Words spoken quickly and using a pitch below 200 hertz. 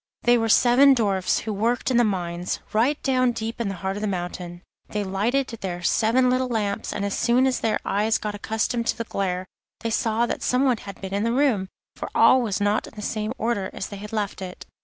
No: fast, 230 wpm; high, 215 Hz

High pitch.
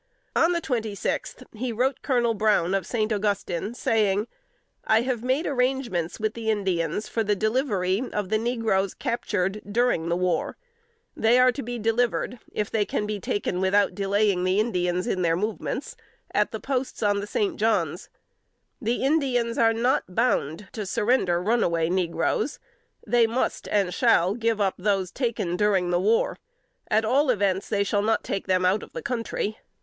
Yes: high, 215 Hz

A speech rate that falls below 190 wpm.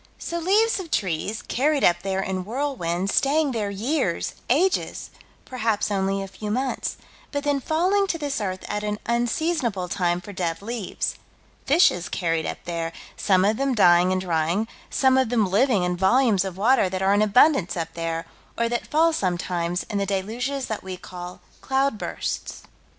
Yes: average, 170 wpm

